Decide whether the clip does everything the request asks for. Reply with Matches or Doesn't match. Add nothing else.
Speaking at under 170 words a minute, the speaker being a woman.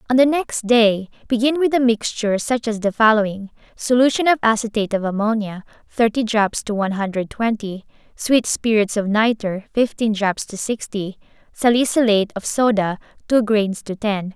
Matches